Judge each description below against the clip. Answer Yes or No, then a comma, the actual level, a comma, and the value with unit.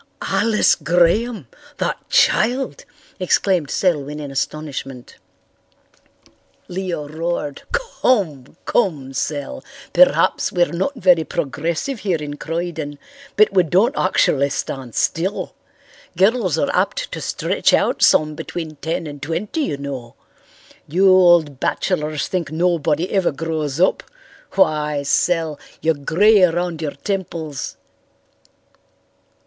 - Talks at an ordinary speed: No, slow, 110 wpm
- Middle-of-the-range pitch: Yes, medium, 165 Hz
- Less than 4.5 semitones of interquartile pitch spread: Yes, average, 4.1 semitones